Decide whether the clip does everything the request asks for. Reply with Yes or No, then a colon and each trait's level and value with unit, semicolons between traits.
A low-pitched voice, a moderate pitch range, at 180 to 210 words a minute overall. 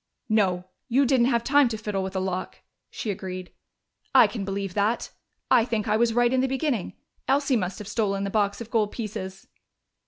No: high, 215 Hz; average, 3.6 semitones; average, 195 wpm